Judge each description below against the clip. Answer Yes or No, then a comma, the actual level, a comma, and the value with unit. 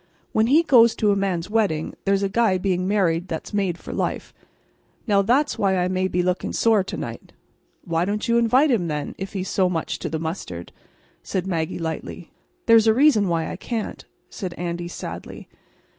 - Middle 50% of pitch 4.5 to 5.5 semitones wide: No, average, 4.0 semitones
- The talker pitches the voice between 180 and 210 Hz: Yes, high, 190 Hz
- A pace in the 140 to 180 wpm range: No, average, 190 wpm